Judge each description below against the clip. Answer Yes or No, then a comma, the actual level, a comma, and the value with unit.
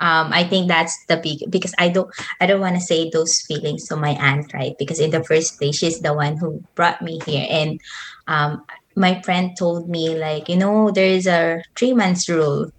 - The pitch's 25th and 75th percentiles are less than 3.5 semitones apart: Yes, average, 2.8 semitones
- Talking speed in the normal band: No, fast, 210 wpm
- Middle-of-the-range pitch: Yes, medium, 165 Hz